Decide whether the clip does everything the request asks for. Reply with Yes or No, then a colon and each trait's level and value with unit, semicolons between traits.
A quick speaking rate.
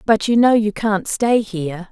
Yes: fast, 220 wpm